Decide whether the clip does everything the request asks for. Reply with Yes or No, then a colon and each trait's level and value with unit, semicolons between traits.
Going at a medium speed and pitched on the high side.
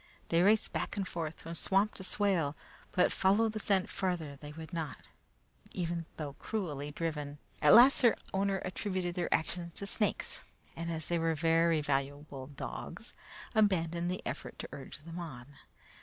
No: average, 165 wpm; medium, 170 Hz